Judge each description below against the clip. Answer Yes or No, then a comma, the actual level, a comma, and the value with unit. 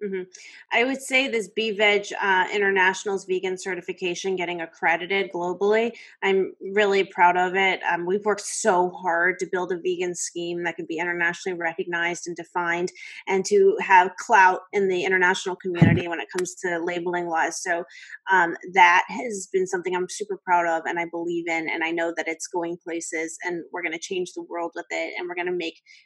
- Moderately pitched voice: Yes, medium, 180 Hz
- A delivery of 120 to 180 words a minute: No, average, 195 wpm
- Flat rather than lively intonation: Yes, narrow, 2.3 semitones